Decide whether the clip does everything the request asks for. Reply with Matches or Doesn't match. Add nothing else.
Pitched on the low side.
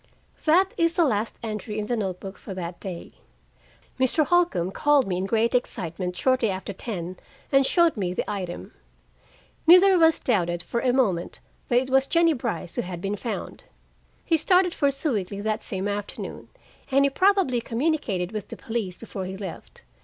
Doesn't match